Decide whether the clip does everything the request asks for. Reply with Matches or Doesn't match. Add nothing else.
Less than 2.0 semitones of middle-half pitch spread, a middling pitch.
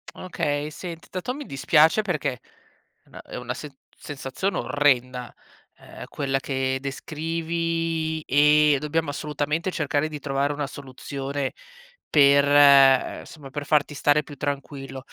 Doesn't match